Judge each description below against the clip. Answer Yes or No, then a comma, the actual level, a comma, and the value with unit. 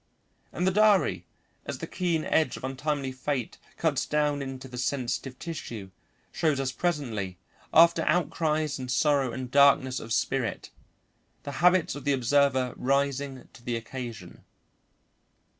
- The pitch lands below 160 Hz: Yes, medium, 140 Hz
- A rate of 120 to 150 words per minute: Yes, average, 140 wpm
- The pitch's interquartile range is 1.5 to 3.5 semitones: Yes, average, 3.0 semitones